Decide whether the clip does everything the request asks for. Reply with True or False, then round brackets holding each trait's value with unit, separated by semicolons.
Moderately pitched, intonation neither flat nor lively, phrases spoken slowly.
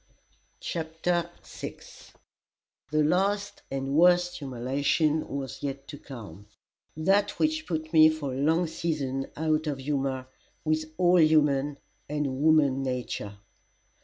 True (150 Hz; 3.2 semitones; 120 wpm)